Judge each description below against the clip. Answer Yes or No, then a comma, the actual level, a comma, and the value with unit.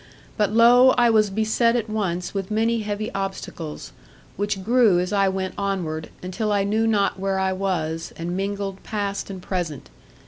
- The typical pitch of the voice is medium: No, high, 195 Hz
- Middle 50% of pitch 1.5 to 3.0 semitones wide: Yes, narrow, 2.6 semitones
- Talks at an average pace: Yes, average, 170 wpm